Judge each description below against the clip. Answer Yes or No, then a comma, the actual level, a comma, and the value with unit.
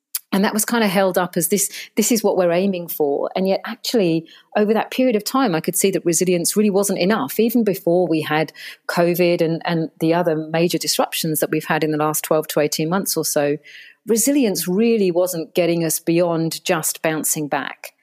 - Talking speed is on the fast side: Yes, fast, 210 wpm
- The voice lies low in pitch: No, medium, 175 Hz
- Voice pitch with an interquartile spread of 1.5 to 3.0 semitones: No, average, 3.8 semitones